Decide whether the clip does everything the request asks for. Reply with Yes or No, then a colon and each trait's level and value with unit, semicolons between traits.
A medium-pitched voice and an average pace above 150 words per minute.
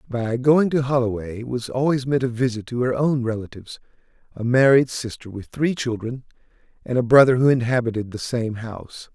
No: low, 125 Hz; average, 170 wpm